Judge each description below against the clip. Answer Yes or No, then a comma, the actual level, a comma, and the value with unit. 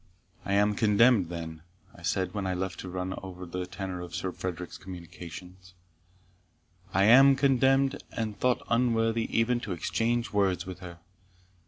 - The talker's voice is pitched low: Yes, very low, 95 Hz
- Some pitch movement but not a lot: Yes, average, 4.1 semitones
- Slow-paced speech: No, average, 150 wpm